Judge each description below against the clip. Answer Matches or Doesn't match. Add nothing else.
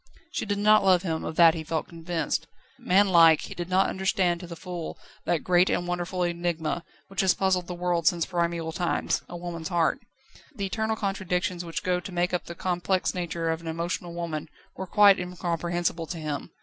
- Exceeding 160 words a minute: Matches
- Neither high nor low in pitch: Matches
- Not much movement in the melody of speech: Matches